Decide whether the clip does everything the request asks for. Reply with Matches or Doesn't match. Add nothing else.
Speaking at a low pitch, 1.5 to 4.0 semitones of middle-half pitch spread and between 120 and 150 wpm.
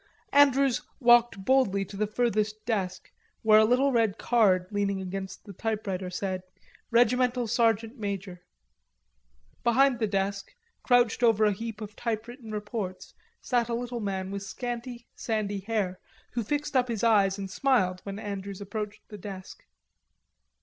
Doesn't match